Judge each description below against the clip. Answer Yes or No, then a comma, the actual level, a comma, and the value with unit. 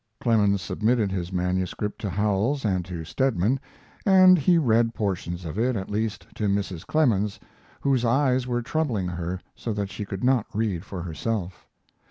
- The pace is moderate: Yes, average, 165 wpm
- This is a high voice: No, low, 105 Hz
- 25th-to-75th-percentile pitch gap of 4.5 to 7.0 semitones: Yes, average, 4.8 semitones